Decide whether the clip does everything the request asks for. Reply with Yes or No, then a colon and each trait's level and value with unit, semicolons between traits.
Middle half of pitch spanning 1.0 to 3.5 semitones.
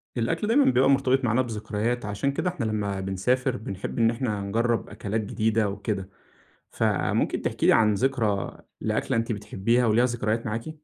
Yes: average, 3.2 semitones